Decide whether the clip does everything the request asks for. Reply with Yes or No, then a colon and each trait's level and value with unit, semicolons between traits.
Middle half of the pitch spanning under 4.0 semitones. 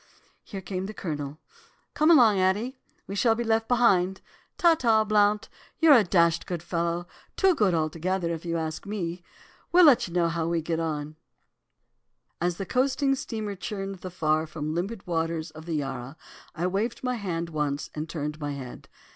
No: average, 5.1 semitones